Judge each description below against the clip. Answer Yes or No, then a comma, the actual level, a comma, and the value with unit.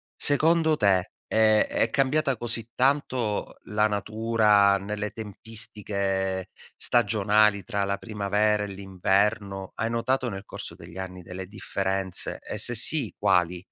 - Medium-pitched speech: No, low, 105 Hz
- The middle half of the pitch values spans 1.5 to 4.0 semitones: Yes, narrow, 2.6 semitones